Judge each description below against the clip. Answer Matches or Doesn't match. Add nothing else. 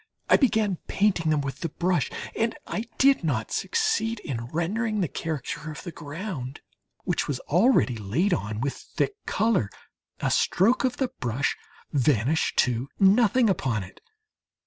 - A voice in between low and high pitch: Matches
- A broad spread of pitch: Matches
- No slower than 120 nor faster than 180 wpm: Matches